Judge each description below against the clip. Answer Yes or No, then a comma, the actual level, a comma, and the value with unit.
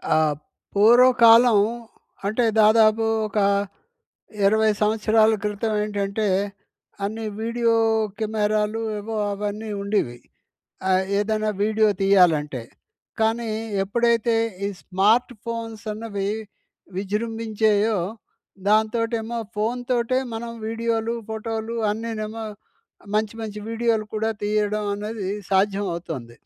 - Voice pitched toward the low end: No, high, 215 Hz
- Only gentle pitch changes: Yes, narrow, 1.7 semitones